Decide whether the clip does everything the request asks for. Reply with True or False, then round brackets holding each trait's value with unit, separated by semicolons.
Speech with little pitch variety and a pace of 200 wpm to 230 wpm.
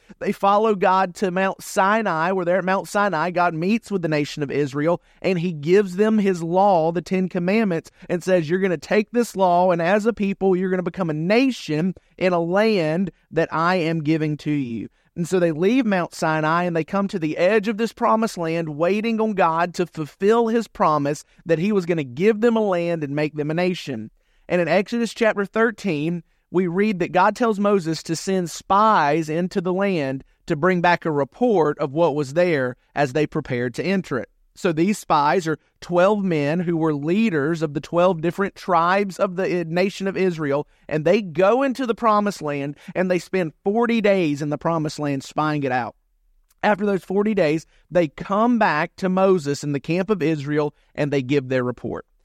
False (4.1 semitones; 205 wpm)